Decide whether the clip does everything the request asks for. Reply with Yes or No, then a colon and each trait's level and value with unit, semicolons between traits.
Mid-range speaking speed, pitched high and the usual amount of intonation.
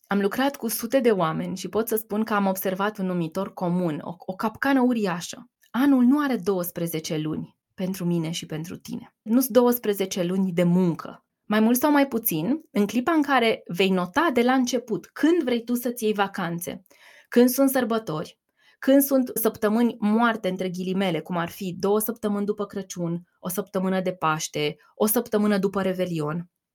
No: fast, 180 wpm; high, 205 Hz; average, 4.8 semitones